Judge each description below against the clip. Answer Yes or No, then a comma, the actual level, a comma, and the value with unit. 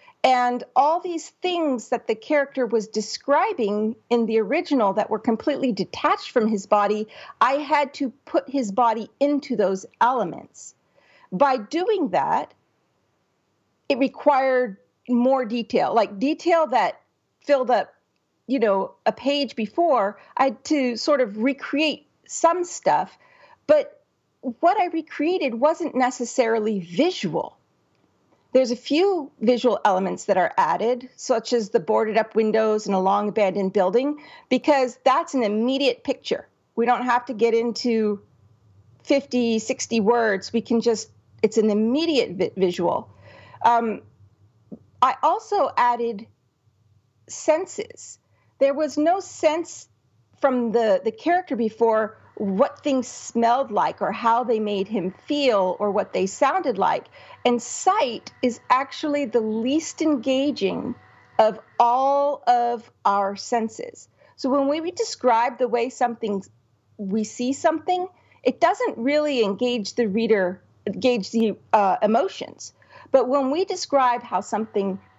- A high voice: Yes, high, 245 Hz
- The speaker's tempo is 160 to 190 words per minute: No, slow, 135 wpm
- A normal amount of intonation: Yes, average, 4.9 semitones